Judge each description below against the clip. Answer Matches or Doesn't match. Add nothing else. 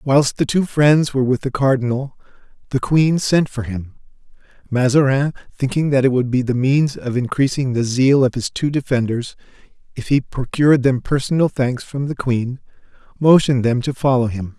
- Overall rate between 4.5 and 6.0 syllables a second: Matches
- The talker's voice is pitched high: Doesn't match